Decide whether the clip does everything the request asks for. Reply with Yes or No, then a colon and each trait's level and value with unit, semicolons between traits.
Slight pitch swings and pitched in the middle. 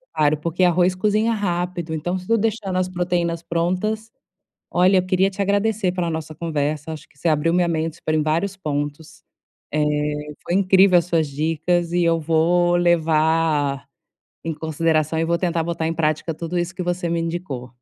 Yes: narrow, 2.3 semitones; medium, 170 Hz